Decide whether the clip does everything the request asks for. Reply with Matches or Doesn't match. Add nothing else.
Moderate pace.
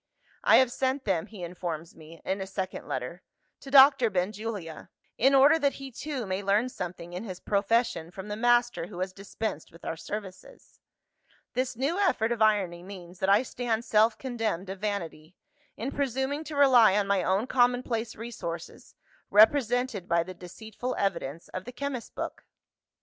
Matches